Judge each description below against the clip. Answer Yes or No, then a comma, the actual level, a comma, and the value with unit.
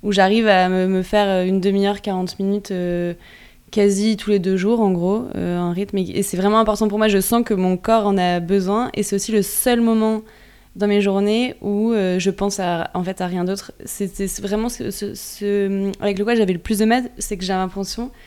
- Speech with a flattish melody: Yes, narrow, 2.1 semitones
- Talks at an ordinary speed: No, fast, 230 wpm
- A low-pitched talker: No, high, 200 Hz